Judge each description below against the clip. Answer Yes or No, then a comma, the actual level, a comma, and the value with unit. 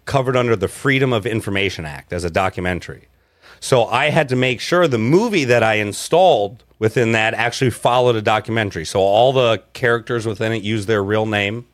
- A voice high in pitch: No, low, 115 Hz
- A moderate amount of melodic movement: Yes, average, 3.3 semitones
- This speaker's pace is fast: No, average, 190 wpm